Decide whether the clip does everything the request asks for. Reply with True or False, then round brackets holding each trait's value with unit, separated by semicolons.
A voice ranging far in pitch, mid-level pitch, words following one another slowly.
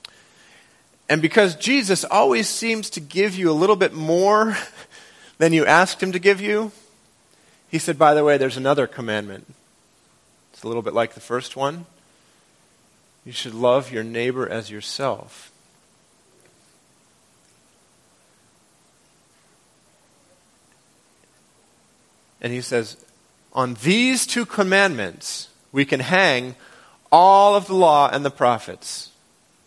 True (8.1 semitones; 155 Hz; 120 wpm)